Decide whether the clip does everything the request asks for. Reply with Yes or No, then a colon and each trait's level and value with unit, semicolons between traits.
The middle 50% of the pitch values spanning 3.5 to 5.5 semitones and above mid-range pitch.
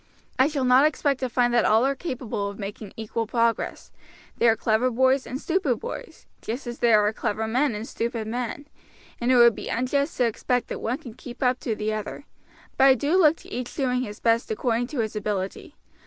No: average, 3.1 semitones; high, 240 Hz